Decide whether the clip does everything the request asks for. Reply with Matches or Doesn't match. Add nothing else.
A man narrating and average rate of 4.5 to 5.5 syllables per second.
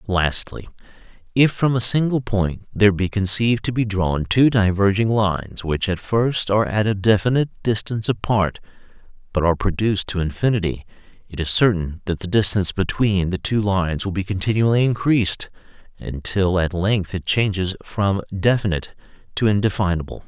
Matches